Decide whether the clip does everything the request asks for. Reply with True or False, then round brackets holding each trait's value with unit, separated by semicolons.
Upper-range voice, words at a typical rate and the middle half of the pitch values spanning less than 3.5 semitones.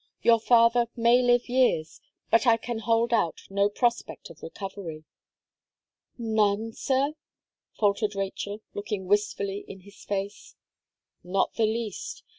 False (215 Hz; 125 wpm; 2.8 semitones)